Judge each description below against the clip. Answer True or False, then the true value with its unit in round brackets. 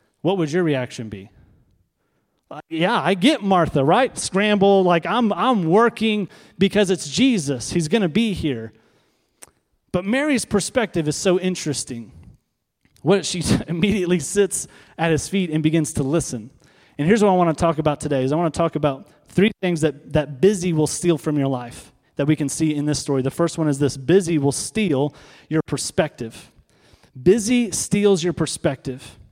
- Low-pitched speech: False (165 Hz)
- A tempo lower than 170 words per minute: False (175 wpm)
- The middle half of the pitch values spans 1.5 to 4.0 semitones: False (5.4 semitones)